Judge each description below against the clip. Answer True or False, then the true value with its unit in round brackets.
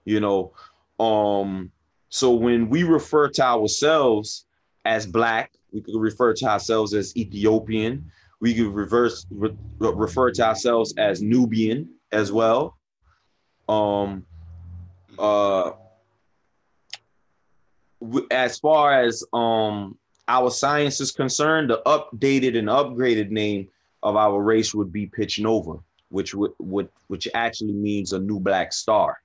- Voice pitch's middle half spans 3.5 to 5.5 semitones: False (2.7 semitones)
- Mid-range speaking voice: False (110 Hz)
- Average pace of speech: False (125 wpm)